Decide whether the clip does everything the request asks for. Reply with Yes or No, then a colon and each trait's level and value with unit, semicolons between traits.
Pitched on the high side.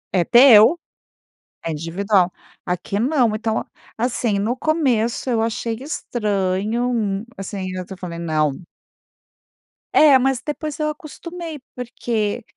Yes: high, 225 Hz